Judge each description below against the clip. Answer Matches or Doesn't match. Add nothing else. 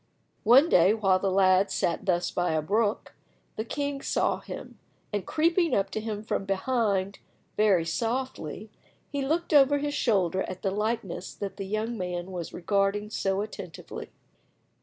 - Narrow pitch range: Doesn't match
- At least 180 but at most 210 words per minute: Doesn't match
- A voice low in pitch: Doesn't match